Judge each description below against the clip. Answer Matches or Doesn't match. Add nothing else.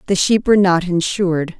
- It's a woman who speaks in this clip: Matches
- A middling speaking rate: Matches